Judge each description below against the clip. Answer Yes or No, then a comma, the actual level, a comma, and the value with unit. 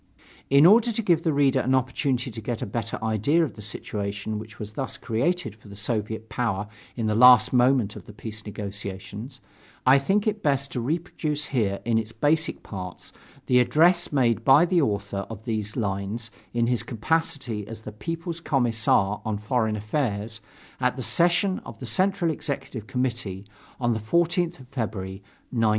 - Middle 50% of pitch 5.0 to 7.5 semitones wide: Yes, average, 5.3 semitones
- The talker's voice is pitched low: Yes, low, 120 Hz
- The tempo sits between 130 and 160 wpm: No, average, 175 wpm